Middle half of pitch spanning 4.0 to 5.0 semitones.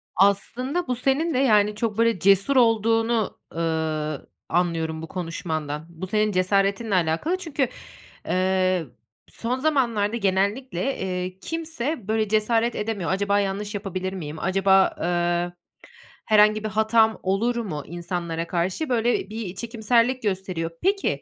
Yes: average, 4.3 semitones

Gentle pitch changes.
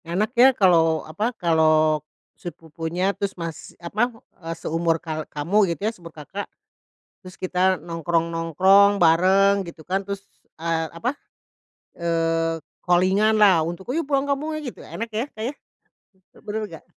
No: average, 3.6 semitones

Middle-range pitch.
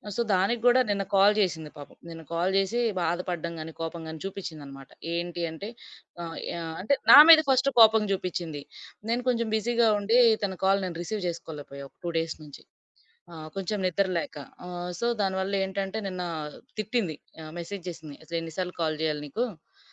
Yes: medium, 180 Hz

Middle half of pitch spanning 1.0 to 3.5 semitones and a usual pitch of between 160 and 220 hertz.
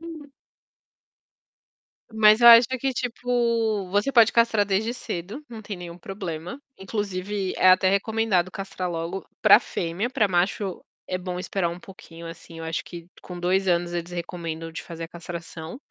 No: average, 4.2 semitones; high, 190 Hz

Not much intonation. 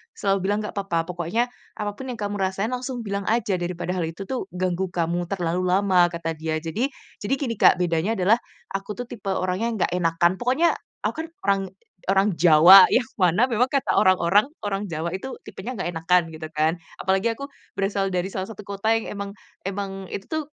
No: average, 3.2 semitones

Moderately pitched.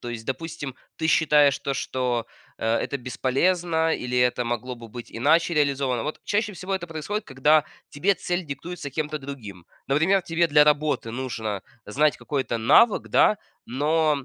Yes: medium, 145 Hz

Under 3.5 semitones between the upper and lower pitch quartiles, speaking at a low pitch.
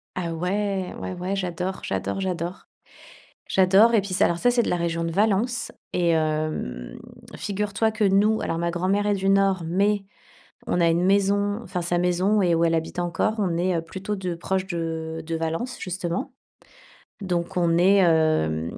No: average, 2.9 semitones; medium, 180 Hz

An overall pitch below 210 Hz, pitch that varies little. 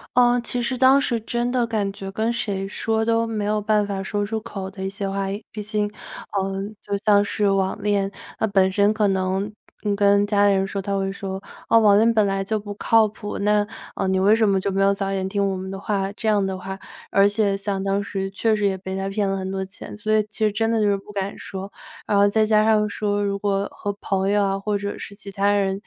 Yes: high, 200 Hz; narrow, 1.5 semitones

